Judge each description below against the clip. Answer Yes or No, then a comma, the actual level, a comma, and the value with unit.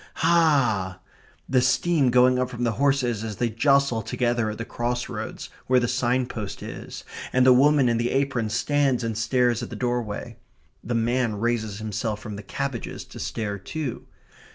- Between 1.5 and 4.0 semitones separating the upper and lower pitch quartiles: Yes, narrow, 2.6 semitones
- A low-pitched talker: Yes, low, 120 Hz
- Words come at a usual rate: Yes, average, 175 wpm